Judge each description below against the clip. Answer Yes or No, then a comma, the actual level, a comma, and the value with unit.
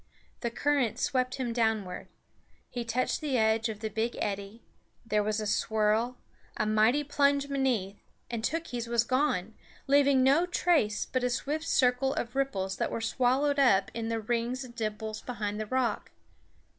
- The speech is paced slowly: No, average, 165 wpm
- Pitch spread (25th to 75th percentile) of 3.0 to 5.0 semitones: Yes, average, 3.6 semitones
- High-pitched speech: Yes, high, 235 Hz